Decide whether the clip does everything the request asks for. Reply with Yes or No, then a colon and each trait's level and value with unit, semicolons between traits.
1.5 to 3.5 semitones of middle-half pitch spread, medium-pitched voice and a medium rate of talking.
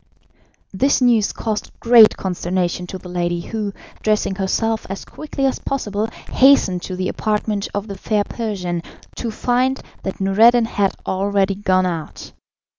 No: average, 3.2 semitones; high, 205 Hz; average, 145 wpm